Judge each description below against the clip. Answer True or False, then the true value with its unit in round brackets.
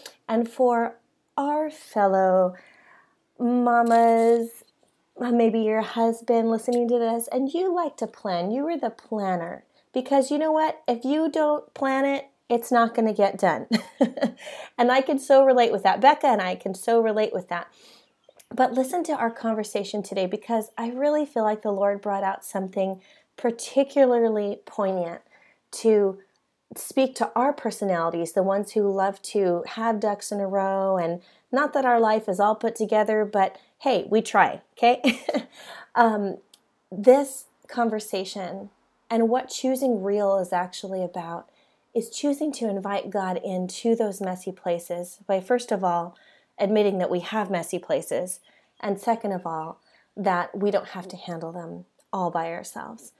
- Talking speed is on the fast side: False (160 wpm)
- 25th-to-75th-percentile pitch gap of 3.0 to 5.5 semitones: True (4.4 semitones)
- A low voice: False (220 Hz)